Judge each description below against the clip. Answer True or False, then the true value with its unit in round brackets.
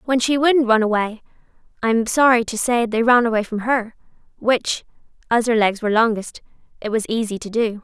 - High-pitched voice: True (230 Hz)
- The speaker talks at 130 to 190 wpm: False (200 wpm)